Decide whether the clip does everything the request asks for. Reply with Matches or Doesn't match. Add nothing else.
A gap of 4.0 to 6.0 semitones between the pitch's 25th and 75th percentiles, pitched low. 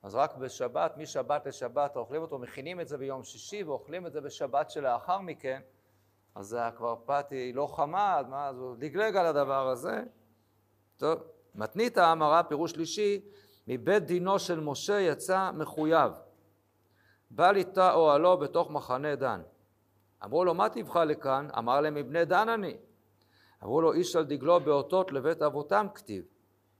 Doesn't match